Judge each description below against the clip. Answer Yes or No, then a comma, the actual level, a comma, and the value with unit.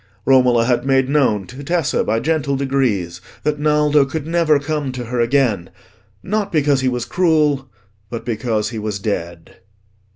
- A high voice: No, low, 135 Hz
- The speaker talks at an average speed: Yes, average, 160 wpm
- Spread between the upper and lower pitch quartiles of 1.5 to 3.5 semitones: No, average, 4.4 semitones